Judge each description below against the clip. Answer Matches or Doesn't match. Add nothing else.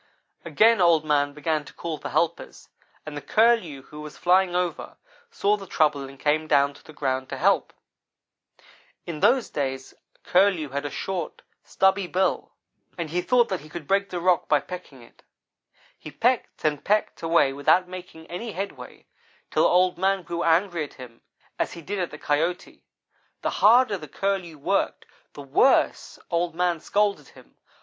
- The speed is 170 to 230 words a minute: Matches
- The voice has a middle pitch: Matches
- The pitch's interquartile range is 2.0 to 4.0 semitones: Doesn't match